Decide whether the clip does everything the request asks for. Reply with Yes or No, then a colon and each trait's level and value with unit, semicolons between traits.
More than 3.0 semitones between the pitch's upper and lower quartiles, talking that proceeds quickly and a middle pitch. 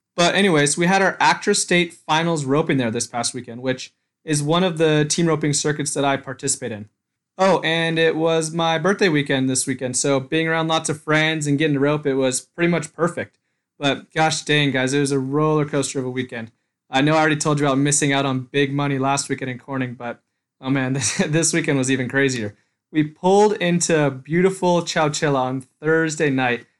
Yes: average, 3.4 semitones; fast, 210 wpm; medium, 145 Hz